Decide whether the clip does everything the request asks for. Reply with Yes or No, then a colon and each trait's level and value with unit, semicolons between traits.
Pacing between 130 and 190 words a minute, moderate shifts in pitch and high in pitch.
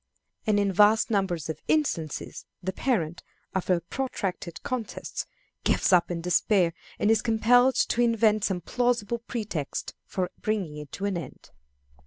Yes: average, 150 wpm; average, 4.7 semitones; high, 200 Hz